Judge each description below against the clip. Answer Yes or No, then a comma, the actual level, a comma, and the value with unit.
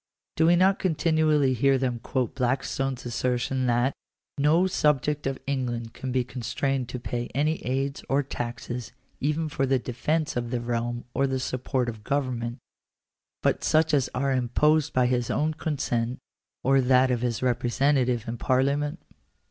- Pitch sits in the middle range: No, low, 130 Hz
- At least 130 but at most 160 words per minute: Yes, average, 155 wpm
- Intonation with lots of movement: No, average, 2.9 semitones